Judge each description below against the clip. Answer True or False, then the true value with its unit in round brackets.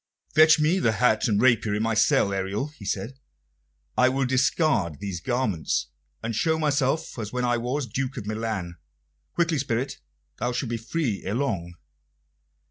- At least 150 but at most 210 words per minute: True (165 wpm)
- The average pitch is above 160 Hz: False (120 Hz)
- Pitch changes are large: False (4.6 semitones)